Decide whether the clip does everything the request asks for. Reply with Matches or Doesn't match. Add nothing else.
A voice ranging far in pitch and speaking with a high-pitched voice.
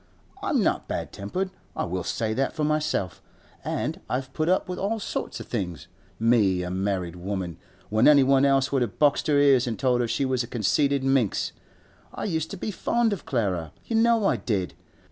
Doesn't match